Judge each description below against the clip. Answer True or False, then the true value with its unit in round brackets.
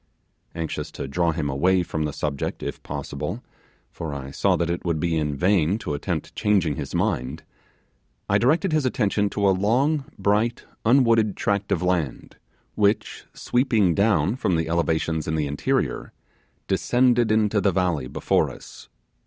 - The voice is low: True (90 Hz)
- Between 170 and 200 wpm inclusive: False (160 wpm)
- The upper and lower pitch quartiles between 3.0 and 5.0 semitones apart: False (5.5 semitones)